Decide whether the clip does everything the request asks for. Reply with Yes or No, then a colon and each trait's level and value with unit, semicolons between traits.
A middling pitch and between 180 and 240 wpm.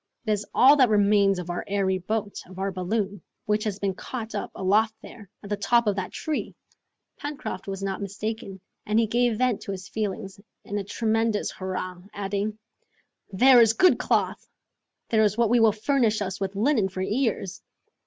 No: high, 205 Hz; average, 185 wpm